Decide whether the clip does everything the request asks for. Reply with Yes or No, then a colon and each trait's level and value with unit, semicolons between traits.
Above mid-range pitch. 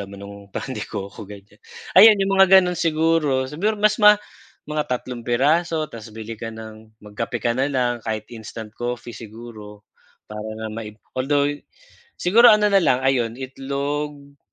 No: low, 130 Hz